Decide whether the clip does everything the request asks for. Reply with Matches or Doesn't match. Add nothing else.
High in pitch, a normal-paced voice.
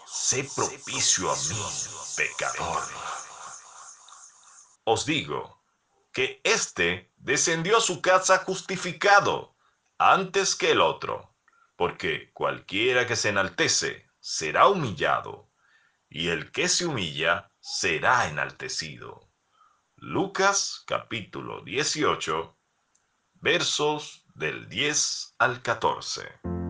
Doesn't match